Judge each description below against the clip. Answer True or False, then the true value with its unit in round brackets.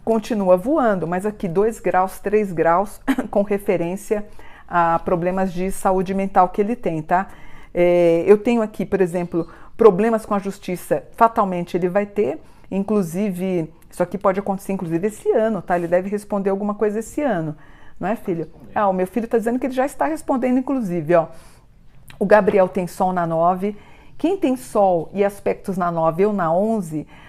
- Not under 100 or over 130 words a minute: False (180 wpm)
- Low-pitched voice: False (195 Hz)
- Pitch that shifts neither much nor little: True (3.1 semitones)